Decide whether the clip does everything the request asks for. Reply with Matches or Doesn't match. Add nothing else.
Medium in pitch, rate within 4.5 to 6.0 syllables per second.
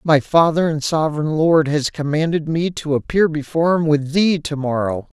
Matches